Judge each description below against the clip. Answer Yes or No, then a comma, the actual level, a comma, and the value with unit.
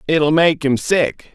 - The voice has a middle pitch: Yes, medium, 150 Hz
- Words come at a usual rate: Yes, average, 180 wpm